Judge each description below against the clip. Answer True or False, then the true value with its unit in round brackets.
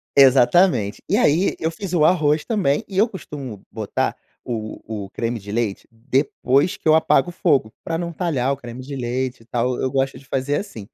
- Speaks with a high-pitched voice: False (135 Hz)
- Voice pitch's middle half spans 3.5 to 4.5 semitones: False (5.3 semitones)